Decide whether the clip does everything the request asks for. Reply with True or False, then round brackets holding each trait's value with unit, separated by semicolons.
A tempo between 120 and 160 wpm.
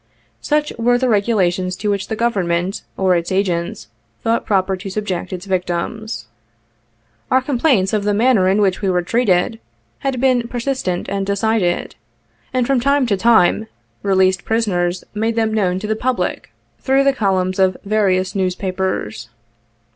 True (155 wpm)